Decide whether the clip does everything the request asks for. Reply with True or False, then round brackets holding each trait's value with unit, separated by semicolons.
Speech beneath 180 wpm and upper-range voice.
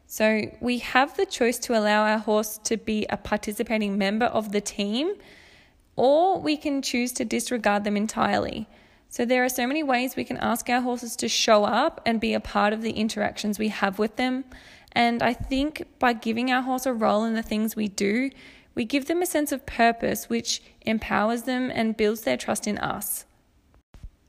False (200 wpm; 230 Hz)